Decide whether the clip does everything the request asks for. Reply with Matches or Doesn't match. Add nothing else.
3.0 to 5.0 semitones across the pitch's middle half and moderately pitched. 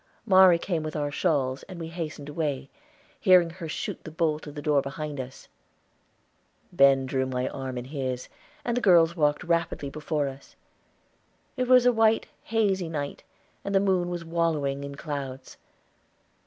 Matches